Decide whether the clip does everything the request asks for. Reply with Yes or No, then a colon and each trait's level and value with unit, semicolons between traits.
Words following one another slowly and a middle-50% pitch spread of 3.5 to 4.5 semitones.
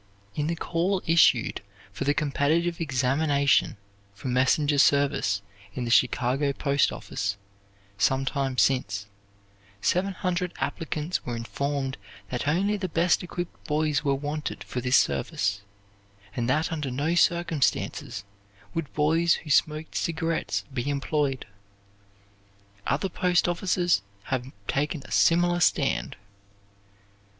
Yes: slow, 120 wpm; average, 4.1 semitones